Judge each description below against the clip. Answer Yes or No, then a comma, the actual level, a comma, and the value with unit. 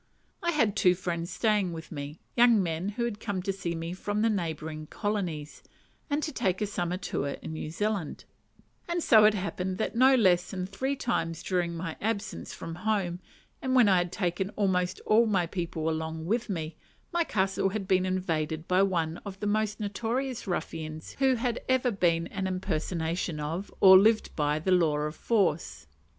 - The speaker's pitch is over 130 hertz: Yes, medium, 185 Hz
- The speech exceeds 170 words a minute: Yes, average, 185 wpm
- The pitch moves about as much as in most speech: Yes, average, 4.3 semitones